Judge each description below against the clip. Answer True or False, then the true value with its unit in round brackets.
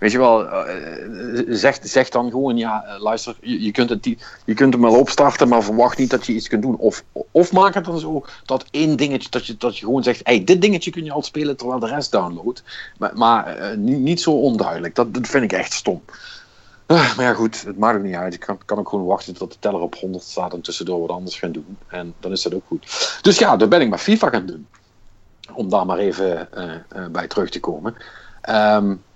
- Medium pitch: False (125 Hz)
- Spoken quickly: True (240 wpm)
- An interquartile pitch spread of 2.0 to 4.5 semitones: False (5.3 semitones)